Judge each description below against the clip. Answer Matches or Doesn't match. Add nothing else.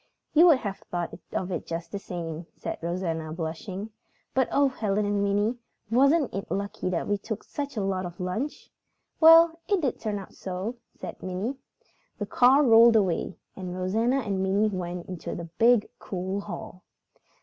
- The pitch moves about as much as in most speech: Matches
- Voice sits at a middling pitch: Doesn't match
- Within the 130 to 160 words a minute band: Doesn't match